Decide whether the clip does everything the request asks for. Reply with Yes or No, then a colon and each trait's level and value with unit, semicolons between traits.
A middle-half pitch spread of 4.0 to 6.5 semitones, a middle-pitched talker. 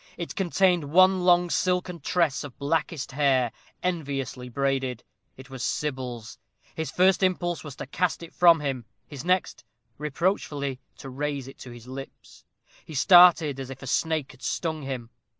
Yes: average, 4.6 semitones; medium, 145 Hz